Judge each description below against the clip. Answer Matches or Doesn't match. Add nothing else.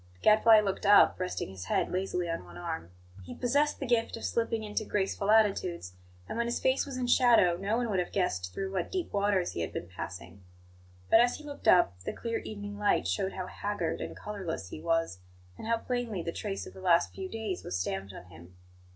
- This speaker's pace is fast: Matches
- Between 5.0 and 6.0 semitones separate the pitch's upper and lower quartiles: Matches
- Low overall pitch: Doesn't match